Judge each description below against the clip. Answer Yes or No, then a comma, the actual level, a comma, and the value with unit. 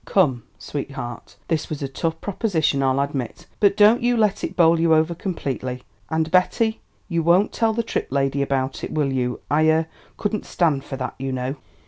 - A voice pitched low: No, medium, 155 Hz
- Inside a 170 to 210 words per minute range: Yes, average, 190 wpm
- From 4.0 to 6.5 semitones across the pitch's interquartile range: Yes, average, 5.2 semitones